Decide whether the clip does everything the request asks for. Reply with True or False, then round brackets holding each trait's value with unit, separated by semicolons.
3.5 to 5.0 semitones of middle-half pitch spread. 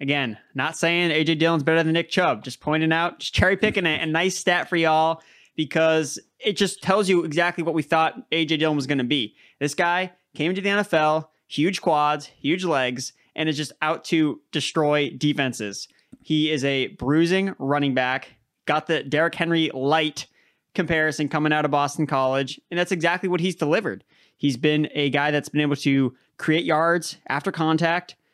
False (2.6 semitones)